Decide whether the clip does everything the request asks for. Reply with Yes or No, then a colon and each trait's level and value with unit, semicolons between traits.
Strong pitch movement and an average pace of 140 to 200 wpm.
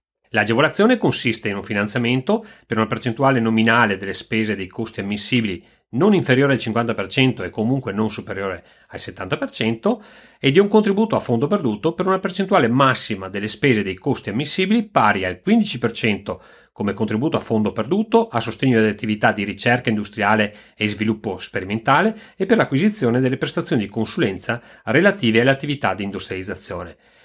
Yes: wide, 6.8 semitones; average, 155 wpm